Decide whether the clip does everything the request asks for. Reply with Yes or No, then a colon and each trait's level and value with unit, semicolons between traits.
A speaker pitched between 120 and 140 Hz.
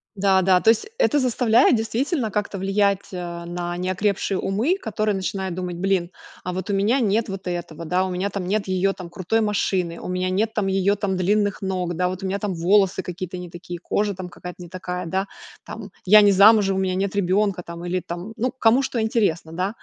No: high, 190 Hz